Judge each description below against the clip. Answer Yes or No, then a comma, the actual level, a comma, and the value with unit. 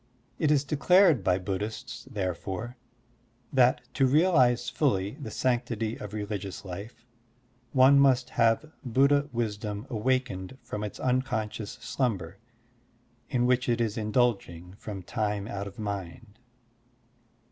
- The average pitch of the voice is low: Yes, low, 115 Hz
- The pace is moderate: No, slow, 120 wpm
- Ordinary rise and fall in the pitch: Yes, average, 4.1 semitones